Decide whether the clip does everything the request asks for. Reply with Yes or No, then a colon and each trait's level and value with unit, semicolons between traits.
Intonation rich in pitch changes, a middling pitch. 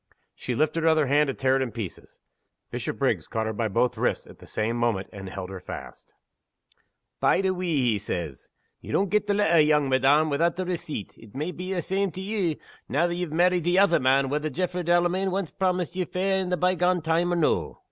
Yes: wide, 5.7 semitones; medium, 165 Hz